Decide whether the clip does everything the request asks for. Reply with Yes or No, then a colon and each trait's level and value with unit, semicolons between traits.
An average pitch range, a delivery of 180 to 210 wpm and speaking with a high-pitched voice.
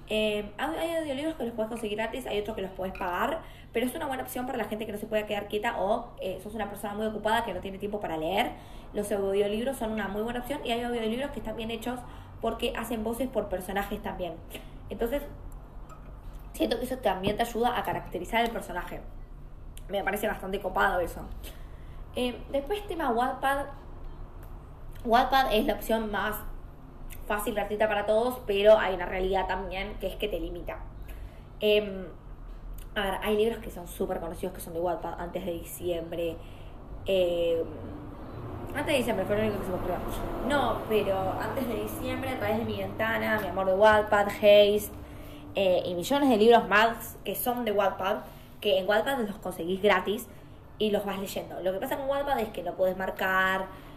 Yes: average, 3.2 semitones; fast, 190 wpm; high, 210 Hz